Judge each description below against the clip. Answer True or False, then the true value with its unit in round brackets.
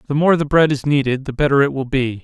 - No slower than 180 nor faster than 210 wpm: False (295 wpm)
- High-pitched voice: False (140 Hz)